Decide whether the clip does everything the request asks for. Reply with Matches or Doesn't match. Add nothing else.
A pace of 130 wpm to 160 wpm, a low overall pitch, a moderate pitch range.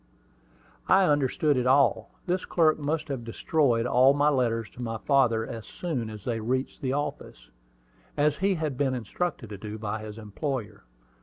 Doesn't match